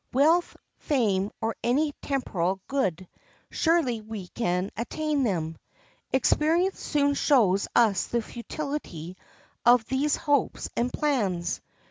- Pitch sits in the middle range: No, high, 240 Hz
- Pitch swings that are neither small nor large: No, wide, 7.0 semitones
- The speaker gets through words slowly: Yes, slow, 105 wpm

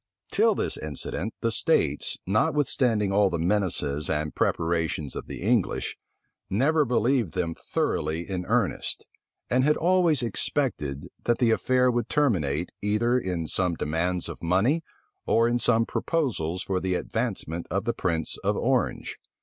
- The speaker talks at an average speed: Yes, average, 145 wpm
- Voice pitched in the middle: No, low, 100 Hz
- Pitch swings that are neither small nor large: No, wide, 6.4 semitones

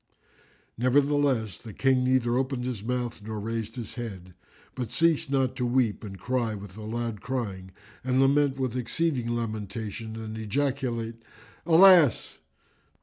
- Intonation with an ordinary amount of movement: Yes, average, 3.2 semitones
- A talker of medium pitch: No, low, 120 Hz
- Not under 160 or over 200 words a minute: No, average, 140 wpm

